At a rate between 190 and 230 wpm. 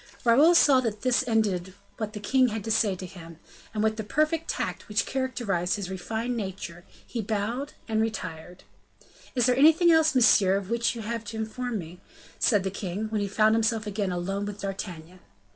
Yes: average, 195 wpm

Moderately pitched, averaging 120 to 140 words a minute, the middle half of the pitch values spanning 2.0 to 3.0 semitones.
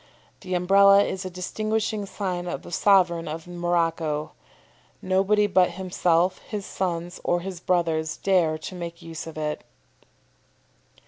Yes: medium, 180 Hz; slow, 135 wpm; narrow, 2.4 semitones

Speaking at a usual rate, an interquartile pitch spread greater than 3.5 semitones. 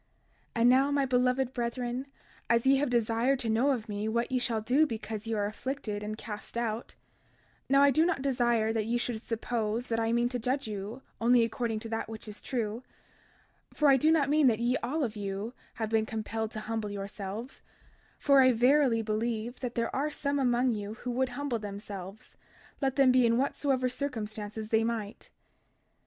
No: average, 195 wpm; average, 2.9 semitones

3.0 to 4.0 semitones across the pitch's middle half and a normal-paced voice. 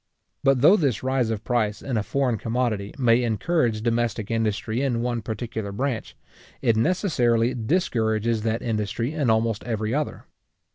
No: narrow, 2.6 semitones; average, 150 wpm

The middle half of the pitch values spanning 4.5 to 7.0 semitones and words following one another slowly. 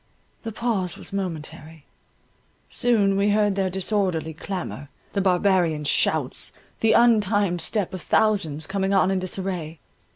No: average, 3.0 semitones; slow, 130 wpm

